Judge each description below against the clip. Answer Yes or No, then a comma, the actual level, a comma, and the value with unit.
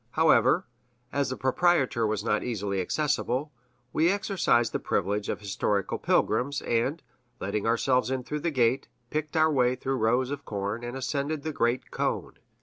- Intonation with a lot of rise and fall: No, average, 4.0 semitones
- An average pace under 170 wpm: Yes, average, 160 wpm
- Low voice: Yes, low, 130 Hz